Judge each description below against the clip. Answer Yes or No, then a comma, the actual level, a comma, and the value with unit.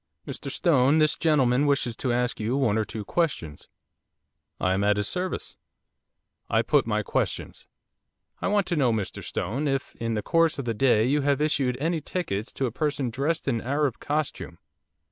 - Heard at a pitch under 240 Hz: Yes, low, 135 Hz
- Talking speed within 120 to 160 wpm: No, average, 185 wpm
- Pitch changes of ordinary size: Yes, average, 4.9 semitones